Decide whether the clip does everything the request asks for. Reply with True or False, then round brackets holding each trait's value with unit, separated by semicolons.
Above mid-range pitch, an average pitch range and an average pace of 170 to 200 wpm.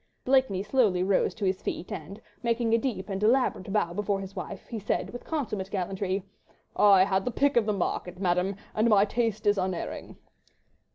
True (200 Hz; 3.2 semitones; 185 wpm)